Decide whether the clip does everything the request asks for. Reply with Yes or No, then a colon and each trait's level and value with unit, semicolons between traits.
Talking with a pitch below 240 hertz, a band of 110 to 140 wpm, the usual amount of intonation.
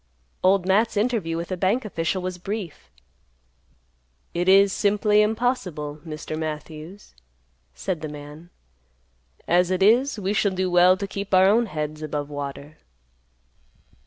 Yes: medium, 185 Hz; slow, 135 wpm; average, 4.6 semitones